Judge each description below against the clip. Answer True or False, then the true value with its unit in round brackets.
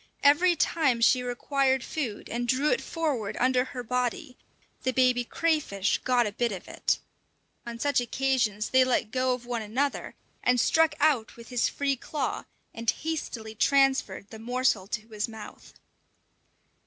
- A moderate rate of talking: True (155 wpm)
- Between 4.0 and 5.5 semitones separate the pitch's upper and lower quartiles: False (3.2 semitones)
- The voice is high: True (250 Hz)